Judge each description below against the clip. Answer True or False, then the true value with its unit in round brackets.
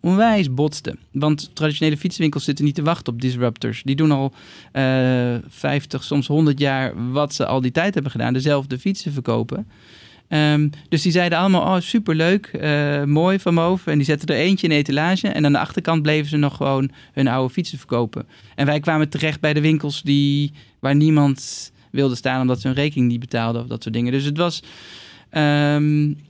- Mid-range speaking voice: True (145 Hz)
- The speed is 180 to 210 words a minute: True (195 wpm)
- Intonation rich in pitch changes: False (3.0 semitones)